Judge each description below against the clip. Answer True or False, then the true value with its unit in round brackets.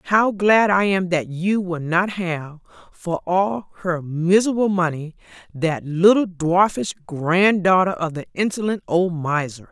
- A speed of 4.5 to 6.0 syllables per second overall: False (4.0 syllables/s)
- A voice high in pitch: False (180 Hz)